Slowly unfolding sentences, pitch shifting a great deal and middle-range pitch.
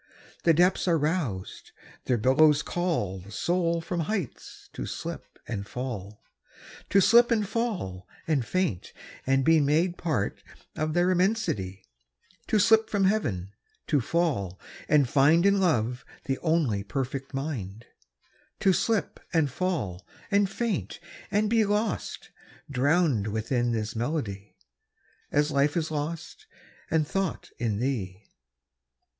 Yes: slow, 115 wpm; wide, 8.6 semitones; medium, 150 Hz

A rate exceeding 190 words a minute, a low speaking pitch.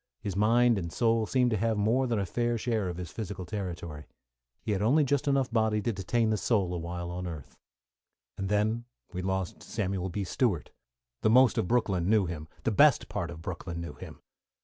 Yes: average, 200 wpm; low, 105 Hz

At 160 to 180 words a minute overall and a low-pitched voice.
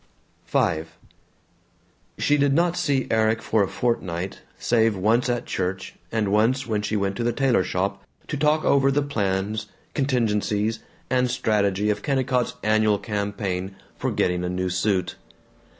No: average, 150 wpm; low, 110 Hz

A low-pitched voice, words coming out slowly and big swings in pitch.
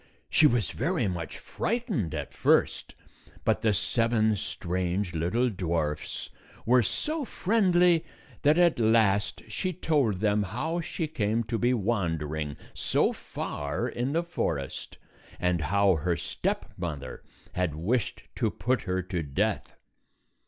Yes: low, 105 Hz; slow, 130 wpm; wide, 7.7 semitones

